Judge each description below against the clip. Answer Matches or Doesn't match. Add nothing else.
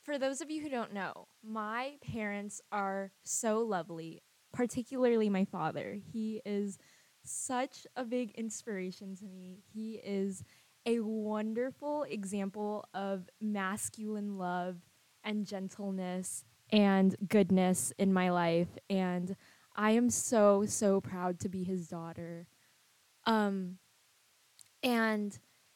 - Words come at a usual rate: Doesn't match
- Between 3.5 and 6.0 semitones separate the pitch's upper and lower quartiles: Doesn't match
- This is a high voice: Matches